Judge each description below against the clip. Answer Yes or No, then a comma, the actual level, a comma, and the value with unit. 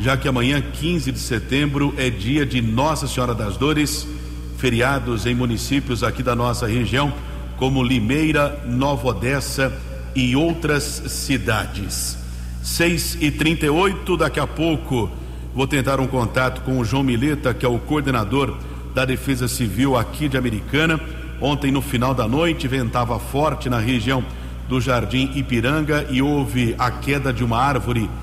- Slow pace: No, average, 150 wpm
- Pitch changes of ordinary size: Yes, average, 3.0 semitones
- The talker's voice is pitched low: Yes, low, 130 Hz